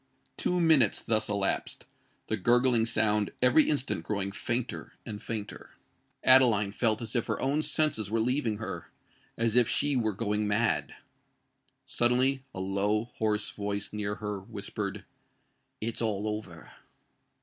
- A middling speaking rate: No, slow, 130 wpm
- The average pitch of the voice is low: Yes, low, 110 Hz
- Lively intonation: No, average, 3.0 semitones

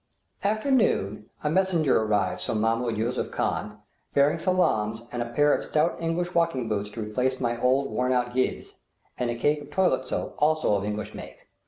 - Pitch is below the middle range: Yes, low, 125 Hz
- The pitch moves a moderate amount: No, wide, 5.9 semitones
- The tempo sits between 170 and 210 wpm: Yes, average, 185 wpm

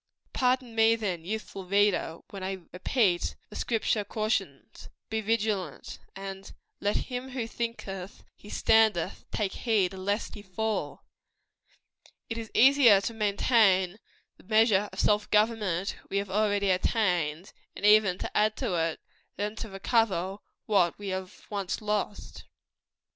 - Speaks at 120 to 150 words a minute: Yes, slow, 135 wpm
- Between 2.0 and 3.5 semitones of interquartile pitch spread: Yes, average, 2.7 semitones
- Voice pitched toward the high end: Yes, high, 205 Hz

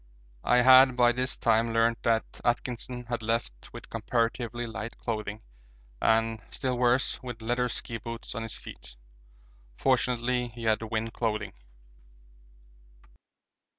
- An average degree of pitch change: No, narrow, 1.5 semitones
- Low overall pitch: Yes, low, 115 Hz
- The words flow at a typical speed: No, slow, 125 wpm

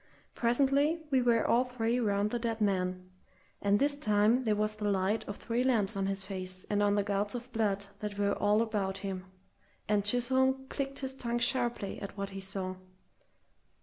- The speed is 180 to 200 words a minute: Yes, average, 185 wpm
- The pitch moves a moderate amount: Yes, average, 3.6 semitones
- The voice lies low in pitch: No, high, 210 Hz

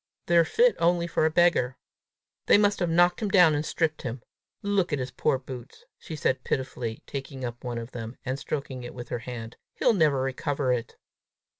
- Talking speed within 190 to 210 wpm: Yes, average, 195 wpm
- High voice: No, medium, 140 Hz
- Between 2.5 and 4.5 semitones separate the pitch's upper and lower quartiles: No, wide, 5.4 semitones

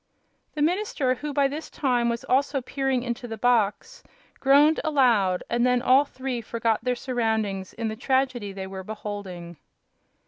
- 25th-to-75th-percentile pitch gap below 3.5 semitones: No, average, 3.8 semitones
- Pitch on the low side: No, high, 245 Hz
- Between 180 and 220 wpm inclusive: No, average, 160 wpm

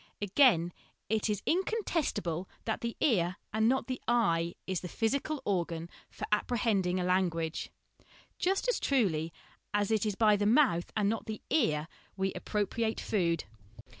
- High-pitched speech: Yes, high, 205 Hz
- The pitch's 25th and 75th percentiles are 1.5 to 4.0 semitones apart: No, average, 5.0 semitones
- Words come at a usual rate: Yes, average, 150 wpm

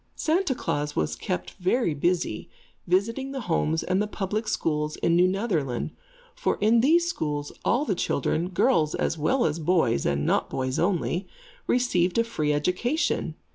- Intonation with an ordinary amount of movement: No, wide, 7.3 semitones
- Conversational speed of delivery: Yes, average, 160 wpm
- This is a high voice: No, medium, 180 Hz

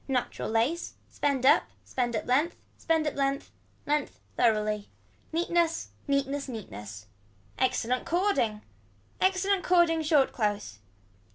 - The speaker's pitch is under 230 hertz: No, very high, 275 Hz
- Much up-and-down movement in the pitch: Yes, wide, 6.5 semitones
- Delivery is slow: Yes, slow, 110 wpm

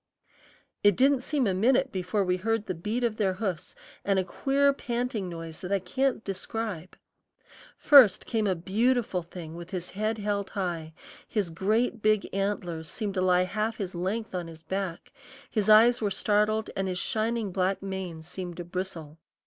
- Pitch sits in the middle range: No, high, 195 Hz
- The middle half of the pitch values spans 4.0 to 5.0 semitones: No, average, 3.6 semitones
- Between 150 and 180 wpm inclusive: Yes, average, 175 wpm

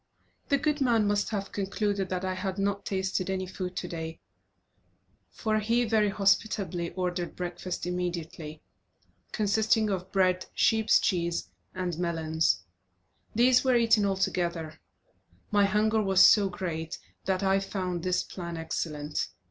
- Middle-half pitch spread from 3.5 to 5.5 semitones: No, average, 2.9 semitones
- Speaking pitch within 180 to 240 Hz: Yes, high, 190 Hz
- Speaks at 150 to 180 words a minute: No, slow, 135 wpm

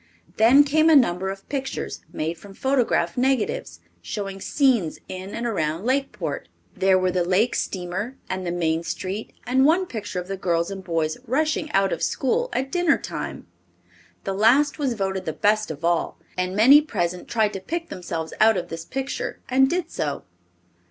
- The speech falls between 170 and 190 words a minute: Yes, average, 180 wpm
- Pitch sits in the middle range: No, high, 200 Hz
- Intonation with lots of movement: Yes, wide, 6.8 semitones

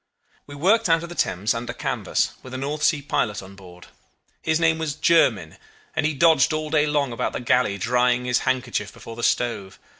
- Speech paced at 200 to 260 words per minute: Yes, fast, 205 wpm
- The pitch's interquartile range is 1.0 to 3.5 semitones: No, average, 5.2 semitones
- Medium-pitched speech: No, low, 130 Hz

